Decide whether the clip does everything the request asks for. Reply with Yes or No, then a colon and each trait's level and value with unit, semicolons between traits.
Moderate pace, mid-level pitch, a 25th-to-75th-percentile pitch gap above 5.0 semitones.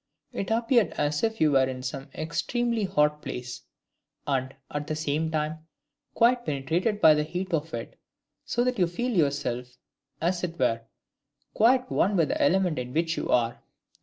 Yes: average, 170 wpm; medium, 160 Hz; wide, 5.5 semitones